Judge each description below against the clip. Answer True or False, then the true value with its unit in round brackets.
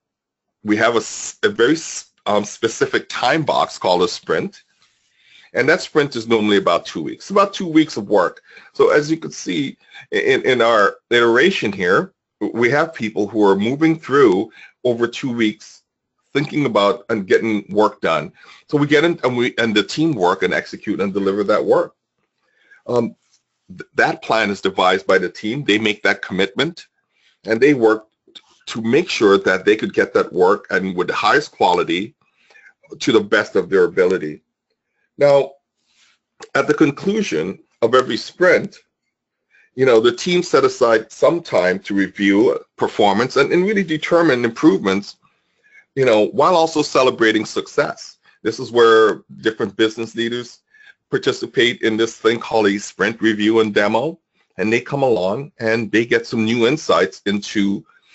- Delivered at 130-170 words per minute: True (165 wpm)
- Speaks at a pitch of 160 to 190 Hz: False (125 Hz)